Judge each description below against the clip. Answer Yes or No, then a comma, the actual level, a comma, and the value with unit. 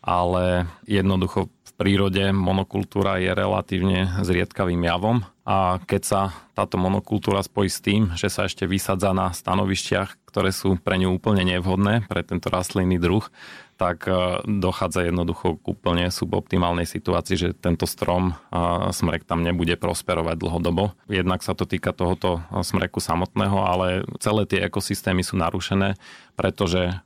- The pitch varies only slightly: Yes, narrow, 1.8 semitones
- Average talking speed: Yes, average, 140 wpm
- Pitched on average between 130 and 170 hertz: No, very low, 95 Hz